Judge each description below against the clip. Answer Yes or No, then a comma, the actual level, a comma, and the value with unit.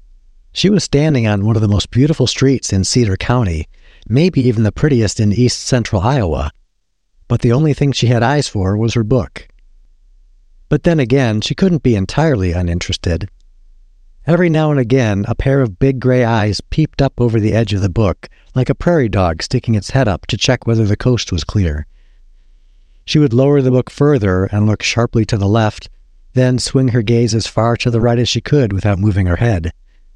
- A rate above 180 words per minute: Yes, average, 200 wpm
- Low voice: Yes, low, 115 Hz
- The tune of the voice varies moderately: No, wide, 5.8 semitones